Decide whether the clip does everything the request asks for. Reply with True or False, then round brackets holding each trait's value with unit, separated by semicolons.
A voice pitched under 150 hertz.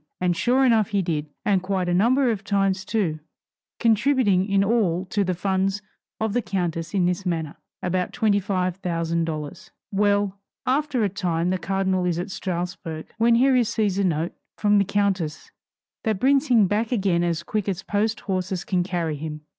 False (195 Hz)